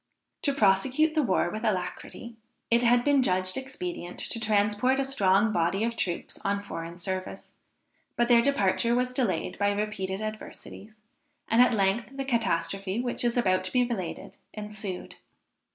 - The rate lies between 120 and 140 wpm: No, average, 155 wpm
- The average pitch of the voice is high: Yes, high, 215 Hz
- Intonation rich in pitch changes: No, average, 4.3 semitones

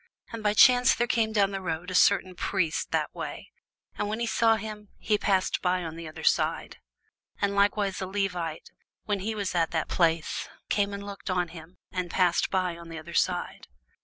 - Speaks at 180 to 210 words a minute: Yes, average, 190 wpm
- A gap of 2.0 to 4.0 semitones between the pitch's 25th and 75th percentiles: Yes, average, 3.2 semitones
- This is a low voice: No, high, 190 Hz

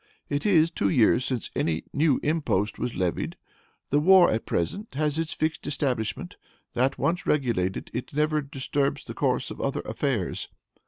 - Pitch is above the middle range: No, medium, 140 Hz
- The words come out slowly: No, average, 160 wpm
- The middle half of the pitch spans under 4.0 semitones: No, average, 4.9 semitones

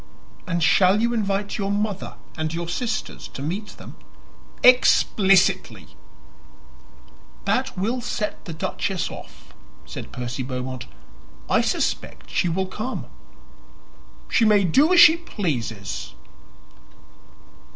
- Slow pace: Yes, slow, 110 wpm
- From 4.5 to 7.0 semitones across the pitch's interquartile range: Yes, average, 5.1 semitones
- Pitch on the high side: Yes, high, 195 Hz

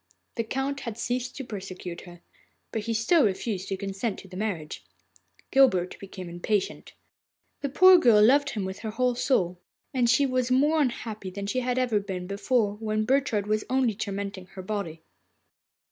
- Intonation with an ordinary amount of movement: Yes, average, 4.6 semitones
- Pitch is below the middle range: No, high, 215 Hz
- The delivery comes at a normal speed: Yes, average, 170 wpm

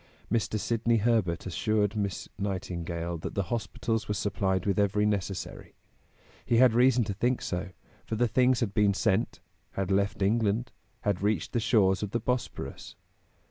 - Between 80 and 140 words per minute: No, average, 160 wpm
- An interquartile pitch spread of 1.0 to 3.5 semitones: Yes, average, 3.2 semitones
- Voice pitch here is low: Yes, low, 105 Hz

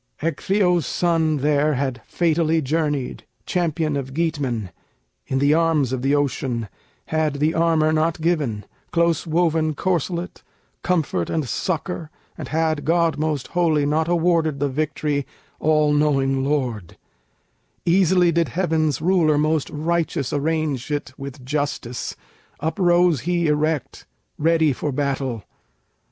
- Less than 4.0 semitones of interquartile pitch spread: Yes, average, 2.8 semitones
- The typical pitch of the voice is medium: Yes, medium, 155 Hz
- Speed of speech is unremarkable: No, slow, 125 wpm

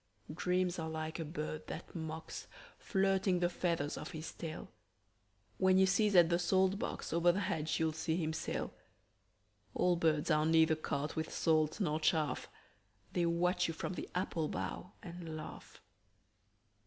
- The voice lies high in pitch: No, medium, 165 Hz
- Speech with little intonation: Yes, narrow, 2.3 semitones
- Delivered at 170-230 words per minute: No, average, 160 wpm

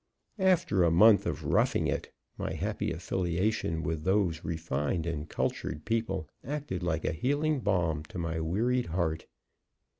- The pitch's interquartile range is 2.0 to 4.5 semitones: No, wide, 5.4 semitones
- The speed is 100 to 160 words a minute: Yes, average, 145 wpm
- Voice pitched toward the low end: Yes, very low, 85 Hz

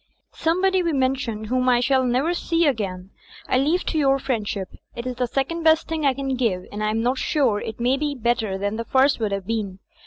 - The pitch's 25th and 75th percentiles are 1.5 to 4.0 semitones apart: No, average, 4.4 semitones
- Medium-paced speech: No, fast, 230 wpm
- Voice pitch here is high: Yes, very high, 255 Hz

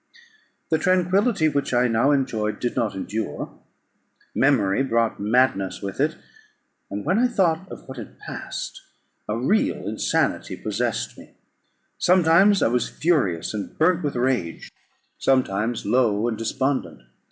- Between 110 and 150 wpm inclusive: Yes, slow, 135 wpm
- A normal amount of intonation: No, wide, 6.9 semitones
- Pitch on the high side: No, low, 130 Hz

